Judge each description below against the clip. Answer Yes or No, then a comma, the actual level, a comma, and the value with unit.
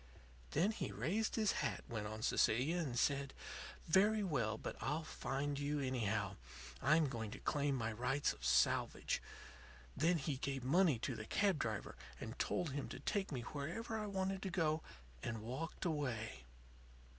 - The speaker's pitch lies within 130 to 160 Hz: Yes, medium, 140 Hz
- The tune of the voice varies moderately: No, wide, 6.1 semitones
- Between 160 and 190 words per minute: Yes, average, 165 wpm